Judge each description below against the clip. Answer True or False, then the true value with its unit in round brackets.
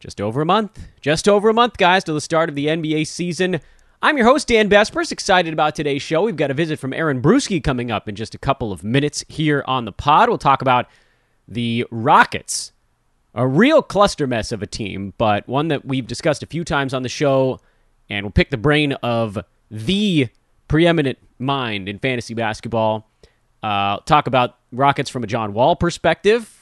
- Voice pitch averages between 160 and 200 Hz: False (140 Hz)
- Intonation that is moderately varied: False (5.8 semitones)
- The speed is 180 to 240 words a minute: True (200 wpm)